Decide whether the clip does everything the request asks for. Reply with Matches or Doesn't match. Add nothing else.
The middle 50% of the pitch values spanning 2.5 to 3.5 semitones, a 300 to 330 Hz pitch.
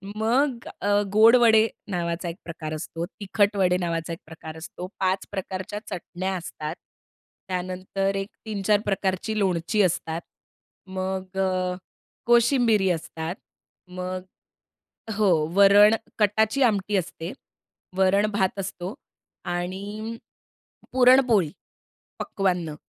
Doesn't match